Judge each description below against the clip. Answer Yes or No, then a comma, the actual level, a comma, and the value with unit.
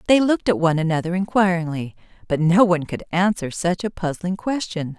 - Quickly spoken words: No, average, 180 wpm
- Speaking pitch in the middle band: Yes, medium, 180 Hz